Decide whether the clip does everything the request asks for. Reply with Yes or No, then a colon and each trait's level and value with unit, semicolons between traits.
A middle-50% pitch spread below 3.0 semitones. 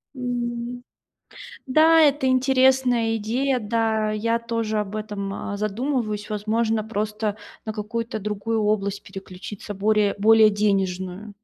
Yes: narrow, 2.4 semitones